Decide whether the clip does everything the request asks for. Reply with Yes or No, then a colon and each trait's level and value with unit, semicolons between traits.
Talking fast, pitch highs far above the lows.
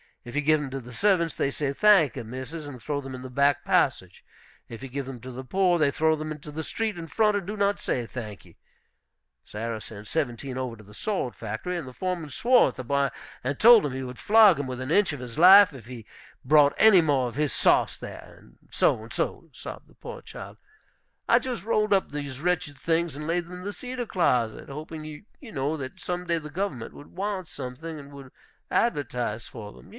Yes: fast, 230 wpm; wide, 5.8 semitones